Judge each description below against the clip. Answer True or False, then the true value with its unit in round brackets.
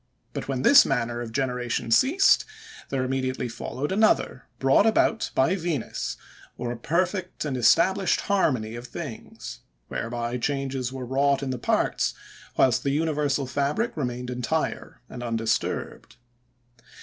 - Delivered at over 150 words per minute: False (135 wpm)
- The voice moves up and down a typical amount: True (4.2 semitones)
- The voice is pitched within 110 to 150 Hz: True (135 Hz)